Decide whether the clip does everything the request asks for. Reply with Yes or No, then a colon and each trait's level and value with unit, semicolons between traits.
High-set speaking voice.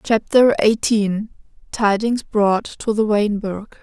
Yes: high, 210 Hz